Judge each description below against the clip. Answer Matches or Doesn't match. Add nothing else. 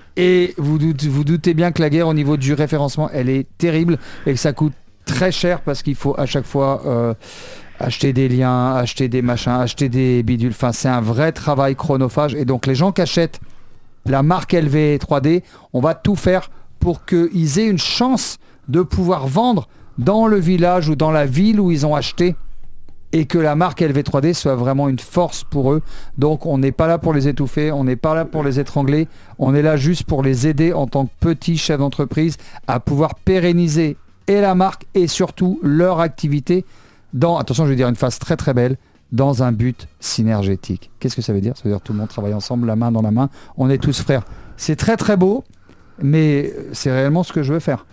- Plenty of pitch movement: Doesn't match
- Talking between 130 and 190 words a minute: Doesn't match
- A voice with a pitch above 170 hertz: Doesn't match